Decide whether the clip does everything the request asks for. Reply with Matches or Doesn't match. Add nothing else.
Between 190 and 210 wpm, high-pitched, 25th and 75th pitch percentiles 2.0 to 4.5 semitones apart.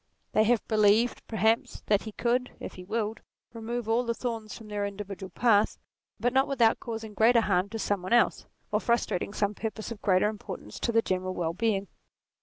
Matches